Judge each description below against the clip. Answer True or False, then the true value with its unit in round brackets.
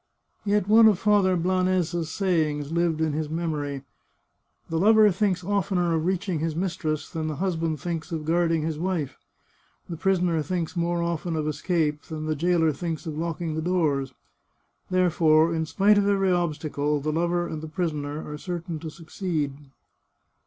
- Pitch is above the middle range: False (165 Hz)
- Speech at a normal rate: True (170 wpm)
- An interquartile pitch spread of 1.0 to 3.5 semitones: True (2.8 semitones)